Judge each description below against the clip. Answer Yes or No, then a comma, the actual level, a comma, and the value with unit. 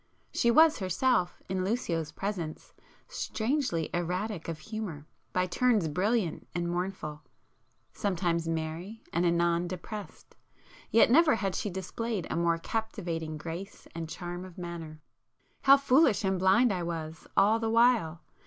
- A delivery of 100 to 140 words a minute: Yes, slow, 135 wpm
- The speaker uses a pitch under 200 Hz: Yes, medium, 185 Hz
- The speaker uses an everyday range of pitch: Yes, average, 4.8 semitones